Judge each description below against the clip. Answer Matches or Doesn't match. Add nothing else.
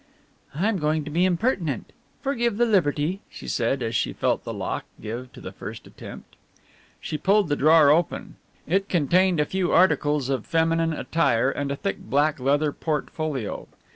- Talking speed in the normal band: Matches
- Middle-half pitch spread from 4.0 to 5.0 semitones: Matches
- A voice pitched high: Doesn't match